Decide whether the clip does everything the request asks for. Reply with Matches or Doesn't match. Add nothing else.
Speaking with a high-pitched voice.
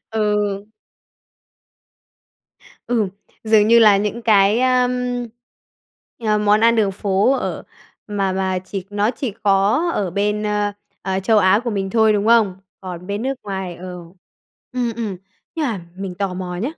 Matches